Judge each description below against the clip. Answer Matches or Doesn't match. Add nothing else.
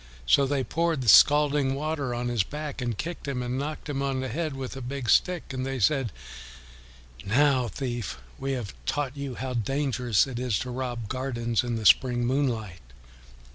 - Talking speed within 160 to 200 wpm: Matches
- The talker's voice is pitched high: Doesn't match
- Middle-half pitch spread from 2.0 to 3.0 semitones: Matches